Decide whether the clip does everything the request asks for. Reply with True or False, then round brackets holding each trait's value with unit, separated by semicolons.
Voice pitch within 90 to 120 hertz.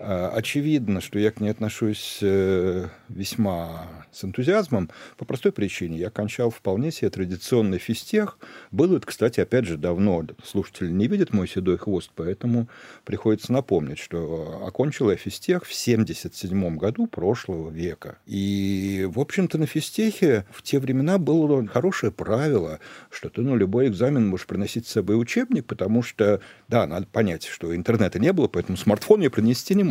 True (105 Hz)